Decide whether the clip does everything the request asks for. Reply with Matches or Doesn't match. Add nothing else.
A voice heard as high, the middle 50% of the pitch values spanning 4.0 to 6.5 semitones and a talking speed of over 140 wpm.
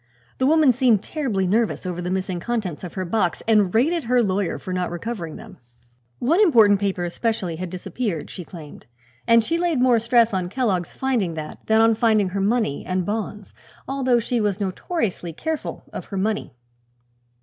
Matches